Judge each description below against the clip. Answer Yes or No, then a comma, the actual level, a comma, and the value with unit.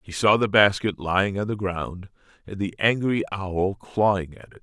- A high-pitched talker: No, low, 100 Hz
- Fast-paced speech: No, average, 195 wpm